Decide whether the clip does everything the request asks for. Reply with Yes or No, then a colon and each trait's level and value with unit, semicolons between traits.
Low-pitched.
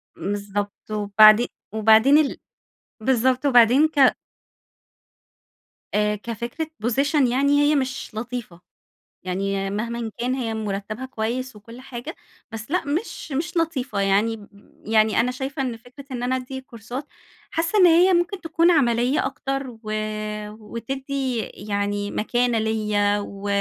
No: high, 240 Hz